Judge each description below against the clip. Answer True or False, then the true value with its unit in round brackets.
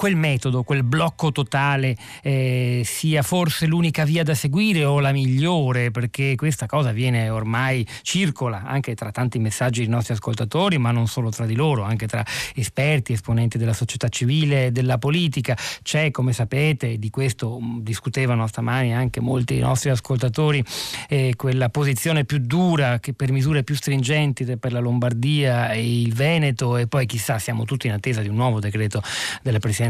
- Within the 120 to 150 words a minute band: False (170 wpm)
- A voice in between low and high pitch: False (130 Hz)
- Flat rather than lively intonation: False (3.2 semitones)